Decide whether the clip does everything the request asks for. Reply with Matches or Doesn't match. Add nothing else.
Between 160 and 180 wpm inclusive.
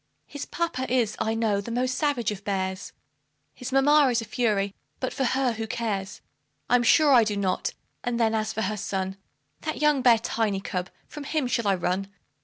Doesn't match